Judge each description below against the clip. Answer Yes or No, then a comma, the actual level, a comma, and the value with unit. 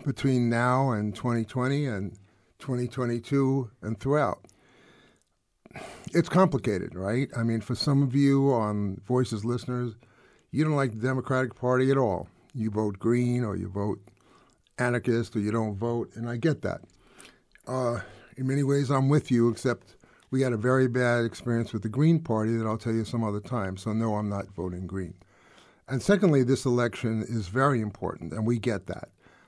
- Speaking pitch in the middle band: No, low, 120 Hz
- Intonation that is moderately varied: Yes, average, 3.2 semitones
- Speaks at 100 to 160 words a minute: No, average, 175 wpm